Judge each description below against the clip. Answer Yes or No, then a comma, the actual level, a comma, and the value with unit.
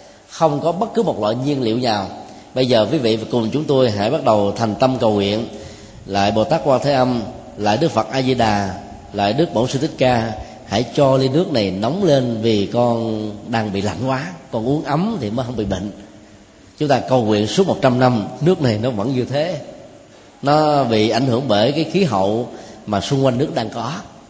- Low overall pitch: Yes, low, 120 Hz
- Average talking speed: Yes, average, 220 wpm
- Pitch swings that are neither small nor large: Yes, average, 4.7 semitones